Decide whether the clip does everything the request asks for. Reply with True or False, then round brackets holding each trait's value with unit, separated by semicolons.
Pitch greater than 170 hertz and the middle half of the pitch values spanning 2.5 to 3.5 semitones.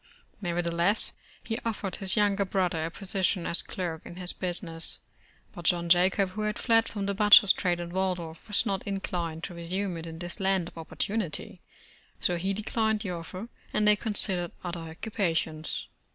True (185 Hz; 2.9 semitones)